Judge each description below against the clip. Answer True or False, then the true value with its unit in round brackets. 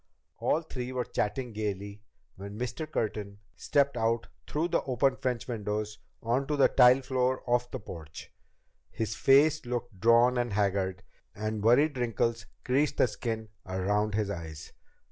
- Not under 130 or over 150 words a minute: True (145 wpm)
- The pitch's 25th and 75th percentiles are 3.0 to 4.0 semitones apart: True (3.6 semitones)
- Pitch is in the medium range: False (115 Hz)